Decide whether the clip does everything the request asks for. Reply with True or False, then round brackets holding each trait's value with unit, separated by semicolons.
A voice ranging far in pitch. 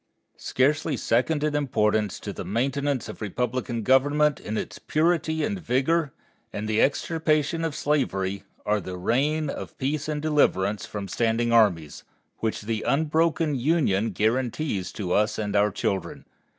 True (6.1 semitones)